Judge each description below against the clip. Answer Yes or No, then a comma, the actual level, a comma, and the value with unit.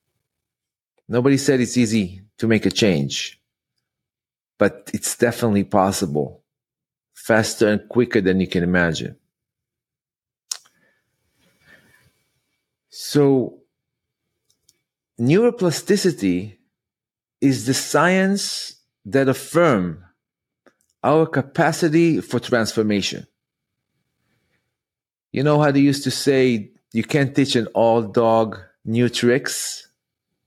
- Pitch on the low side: Yes, low, 120 Hz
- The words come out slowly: Yes, slow, 90 wpm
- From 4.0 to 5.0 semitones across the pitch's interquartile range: No, wide, 5.6 semitones